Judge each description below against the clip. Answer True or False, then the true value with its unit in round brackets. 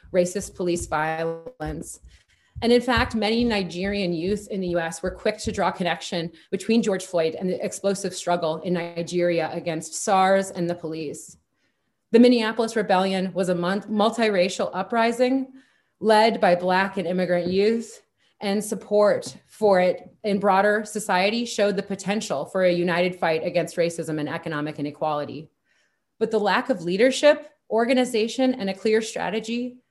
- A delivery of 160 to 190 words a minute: False (145 wpm)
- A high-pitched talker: True (195 Hz)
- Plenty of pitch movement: False (4.1 semitones)